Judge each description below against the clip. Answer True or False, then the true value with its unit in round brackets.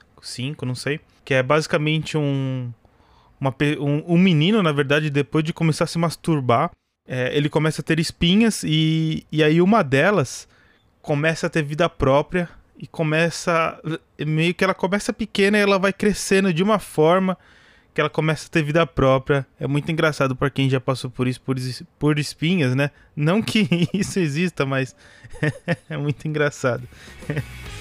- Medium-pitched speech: True (155 Hz)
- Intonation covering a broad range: False (4.1 semitones)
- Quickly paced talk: False (165 wpm)